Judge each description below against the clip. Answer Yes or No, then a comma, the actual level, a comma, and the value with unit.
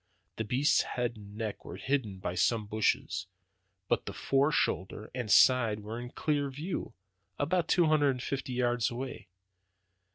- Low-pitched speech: Yes, low, 125 Hz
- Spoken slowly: No, average, 160 wpm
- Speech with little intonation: No, average, 4.5 semitones